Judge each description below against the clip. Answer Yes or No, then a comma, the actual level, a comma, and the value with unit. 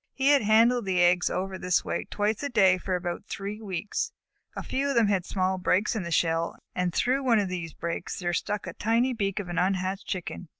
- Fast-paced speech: Yes, fast, 240 wpm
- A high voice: Yes, high, 195 Hz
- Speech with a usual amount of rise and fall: Yes, average, 3.5 semitones